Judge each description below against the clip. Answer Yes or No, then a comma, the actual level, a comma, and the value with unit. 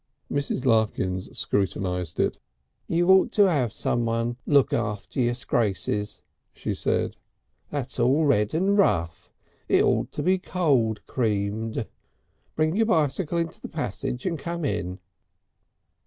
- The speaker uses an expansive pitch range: Yes, wide, 7.3 semitones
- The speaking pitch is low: Yes, low, 125 Hz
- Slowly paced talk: Yes, slow, 130 wpm